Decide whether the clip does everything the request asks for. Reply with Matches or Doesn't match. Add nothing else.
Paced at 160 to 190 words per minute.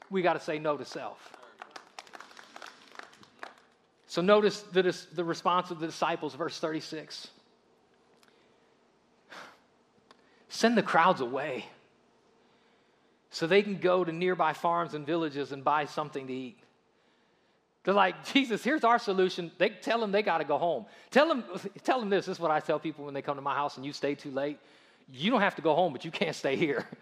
Matches